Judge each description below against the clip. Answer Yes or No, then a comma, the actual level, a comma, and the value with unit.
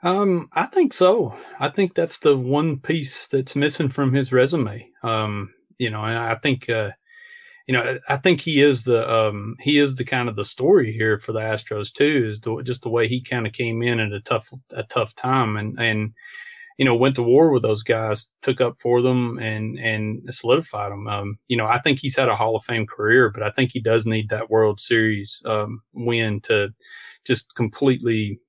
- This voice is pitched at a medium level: No, low, 120 Hz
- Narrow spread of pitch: No, average, 3.8 semitones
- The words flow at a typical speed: No, fast, 215 wpm